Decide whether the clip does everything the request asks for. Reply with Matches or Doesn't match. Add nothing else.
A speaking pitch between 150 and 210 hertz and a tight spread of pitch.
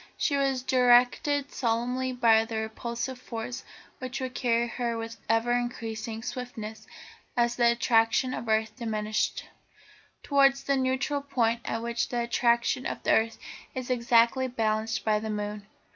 Doesn't match